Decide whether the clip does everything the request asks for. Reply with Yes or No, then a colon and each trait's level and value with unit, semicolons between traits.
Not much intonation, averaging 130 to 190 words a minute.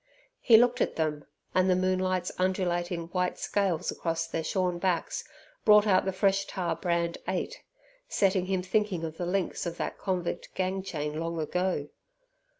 Yes: narrow, 2.0 semitones; average, 160 wpm